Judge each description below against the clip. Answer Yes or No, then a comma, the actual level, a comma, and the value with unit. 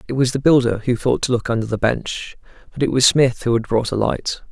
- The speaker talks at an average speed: No, fast, 265 wpm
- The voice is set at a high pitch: No, low, 120 Hz